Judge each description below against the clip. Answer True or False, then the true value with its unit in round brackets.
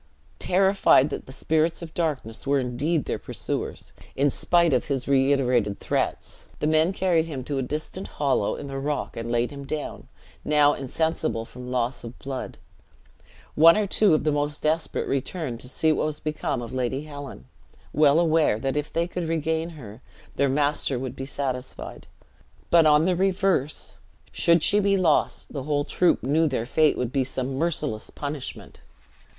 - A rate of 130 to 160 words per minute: False (175 wpm)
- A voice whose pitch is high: False (145 Hz)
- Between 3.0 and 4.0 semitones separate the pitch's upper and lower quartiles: True (3.5 semitones)